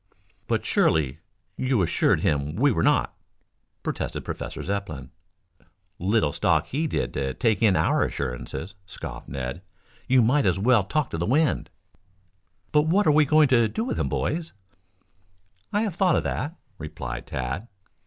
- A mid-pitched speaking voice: No, low, 110 Hz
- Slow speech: No, average, 155 wpm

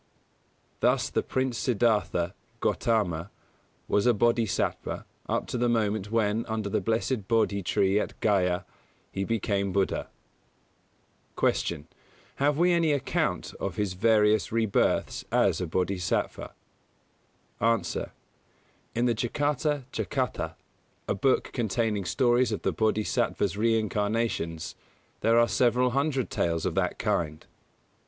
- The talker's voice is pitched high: No, low, 110 Hz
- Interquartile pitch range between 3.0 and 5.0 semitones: Yes, average, 3.4 semitones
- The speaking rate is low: Yes, slow, 120 wpm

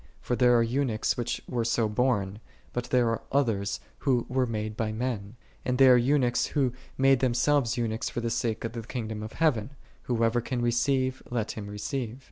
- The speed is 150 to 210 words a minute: Yes, average, 190 wpm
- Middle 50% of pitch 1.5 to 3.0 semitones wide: Yes, narrow, 2.6 semitones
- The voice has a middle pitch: No, low, 120 Hz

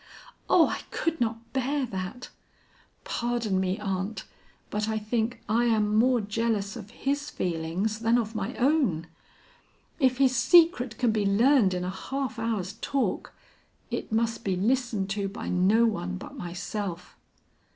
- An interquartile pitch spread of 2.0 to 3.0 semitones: No, average, 3.9 semitones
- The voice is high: Yes, high, 220 Hz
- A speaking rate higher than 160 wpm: No, average, 150 wpm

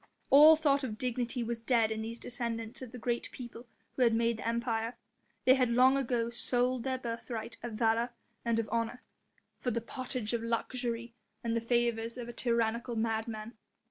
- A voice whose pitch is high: Yes, high, 235 Hz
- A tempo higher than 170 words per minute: Yes, average, 180 wpm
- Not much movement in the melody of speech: Yes, narrow, 1.5 semitones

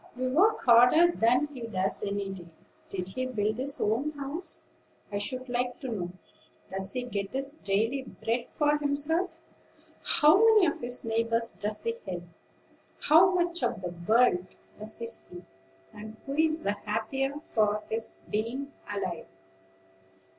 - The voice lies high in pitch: Yes, high, 240 Hz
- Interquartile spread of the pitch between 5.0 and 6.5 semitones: Yes, average, 5.3 semitones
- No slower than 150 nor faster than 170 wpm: Yes, average, 155 wpm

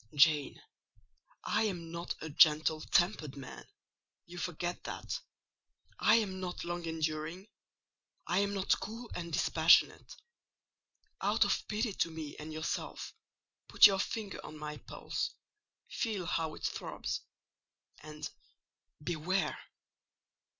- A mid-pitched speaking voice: Yes, medium, 170 Hz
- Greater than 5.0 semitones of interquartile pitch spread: No, average, 3.8 semitones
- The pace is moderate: No, slow, 115 wpm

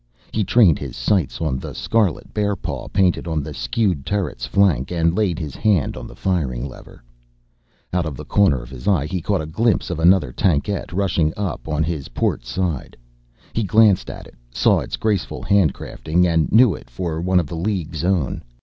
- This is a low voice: Yes, very low, 85 Hz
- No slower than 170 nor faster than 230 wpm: Yes, average, 190 wpm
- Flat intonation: No, average, 4.7 semitones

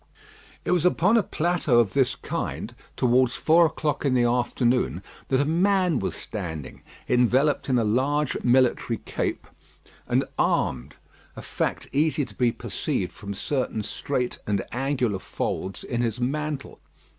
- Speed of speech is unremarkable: Yes, average, 145 wpm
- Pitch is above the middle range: No, low, 125 Hz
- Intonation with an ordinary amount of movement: Yes, average, 4.1 semitones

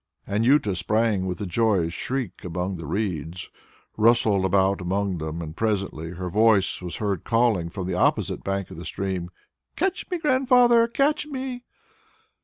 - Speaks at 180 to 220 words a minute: No, average, 155 wpm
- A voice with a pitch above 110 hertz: No, low, 100 Hz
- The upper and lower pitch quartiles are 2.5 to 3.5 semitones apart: No, average, 4.9 semitones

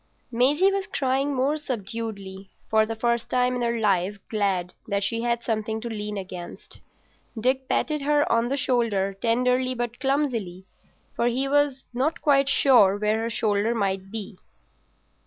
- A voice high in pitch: Yes, high, 235 Hz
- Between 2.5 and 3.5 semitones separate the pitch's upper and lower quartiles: No, average, 4.1 semitones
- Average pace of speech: Yes, average, 155 wpm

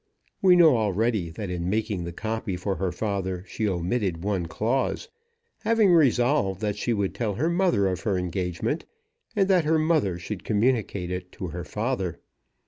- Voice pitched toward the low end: Yes, low, 105 Hz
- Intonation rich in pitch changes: Yes, wide, 5.7 semitones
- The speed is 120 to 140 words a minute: No, average, 170 wpm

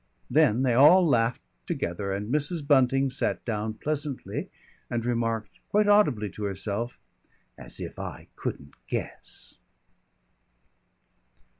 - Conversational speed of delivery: No, slow, 115 wpm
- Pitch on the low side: Yes, low, 120 Hz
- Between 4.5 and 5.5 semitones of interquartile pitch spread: Yes, average, 5.1 semitones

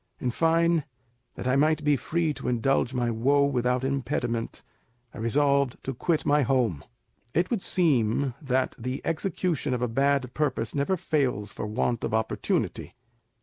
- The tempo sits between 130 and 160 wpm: Yes, average, 155 wpm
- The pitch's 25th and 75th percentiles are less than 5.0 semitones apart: Yes, average, 3.6 semitones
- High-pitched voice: No, low, 135 Hz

